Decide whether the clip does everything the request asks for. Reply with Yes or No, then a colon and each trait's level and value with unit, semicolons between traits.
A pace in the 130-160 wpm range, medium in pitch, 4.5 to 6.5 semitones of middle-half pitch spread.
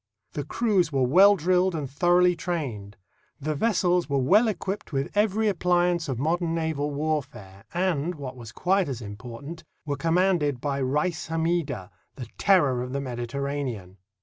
Yes: average, 150 wpm; medium, 155 Hz; average, 4.8 semitones